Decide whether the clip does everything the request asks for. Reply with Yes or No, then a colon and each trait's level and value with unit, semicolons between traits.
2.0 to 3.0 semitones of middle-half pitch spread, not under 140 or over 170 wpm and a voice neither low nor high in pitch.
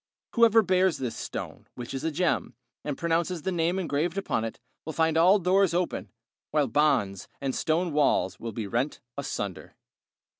No: wide, 5.5 semitones; average, 165 wpm; medium, 160 Hz